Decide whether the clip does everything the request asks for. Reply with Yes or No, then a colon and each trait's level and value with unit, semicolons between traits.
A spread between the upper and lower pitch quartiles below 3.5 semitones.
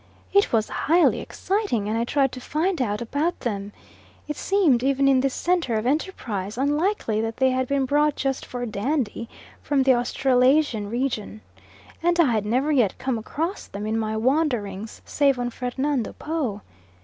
No: average, 4.8 semitones